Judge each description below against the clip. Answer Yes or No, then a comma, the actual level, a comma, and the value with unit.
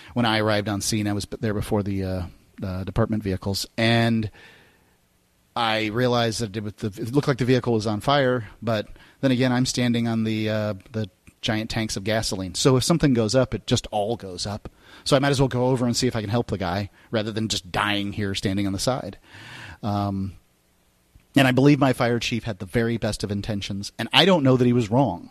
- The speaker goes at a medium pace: No, fast, 225 wpm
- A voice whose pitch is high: No, low, 110 Hz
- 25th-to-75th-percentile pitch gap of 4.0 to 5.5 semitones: No, average, 3.4 semitones